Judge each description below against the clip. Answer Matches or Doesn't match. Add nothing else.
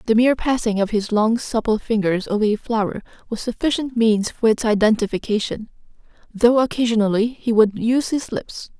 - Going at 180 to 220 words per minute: Doesn't match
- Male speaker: Doesn't match